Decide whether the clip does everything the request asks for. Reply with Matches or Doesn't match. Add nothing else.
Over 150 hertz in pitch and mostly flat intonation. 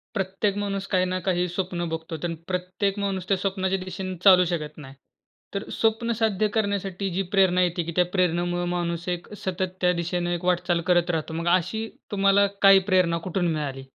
Matches